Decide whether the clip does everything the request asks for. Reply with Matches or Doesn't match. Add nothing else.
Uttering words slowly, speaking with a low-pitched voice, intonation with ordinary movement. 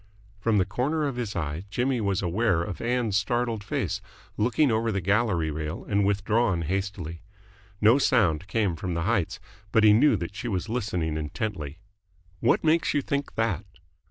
Doesn't match